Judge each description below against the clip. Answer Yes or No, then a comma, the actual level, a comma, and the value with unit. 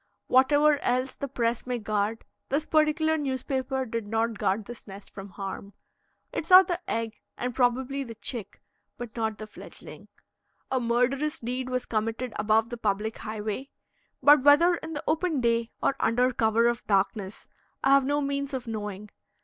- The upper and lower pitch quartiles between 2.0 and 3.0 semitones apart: No, average, 3.9 semitones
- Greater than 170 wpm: No, average, 165 wpm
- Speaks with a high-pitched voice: Yes, high, 245 Hz